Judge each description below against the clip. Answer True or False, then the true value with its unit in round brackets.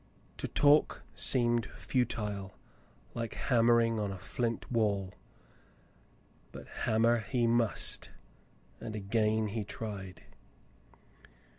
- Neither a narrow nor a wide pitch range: False (2.3 semitones)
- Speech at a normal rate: False (95 wpm)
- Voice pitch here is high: False (115 Hz)